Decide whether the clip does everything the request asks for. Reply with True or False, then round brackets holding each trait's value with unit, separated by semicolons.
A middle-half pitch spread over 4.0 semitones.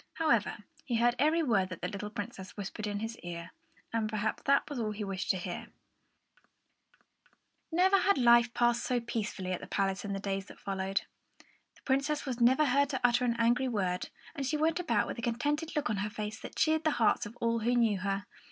True (4.8 semitones)